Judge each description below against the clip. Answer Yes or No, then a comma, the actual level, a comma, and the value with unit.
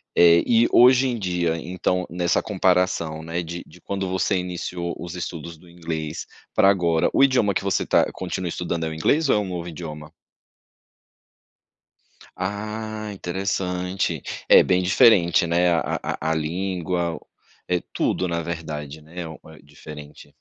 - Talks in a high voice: No, very low, 90 Hz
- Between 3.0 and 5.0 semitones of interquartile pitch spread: No, narrow, 2.6 semitones